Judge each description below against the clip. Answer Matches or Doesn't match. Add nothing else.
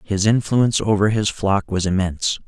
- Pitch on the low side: Matches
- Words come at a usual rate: Matches